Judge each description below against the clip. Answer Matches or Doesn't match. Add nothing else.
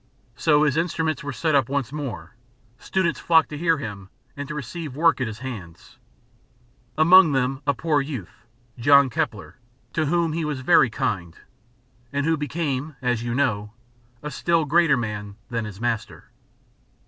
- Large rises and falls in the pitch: Doesn't match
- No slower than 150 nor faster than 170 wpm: Matches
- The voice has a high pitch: Doesn't match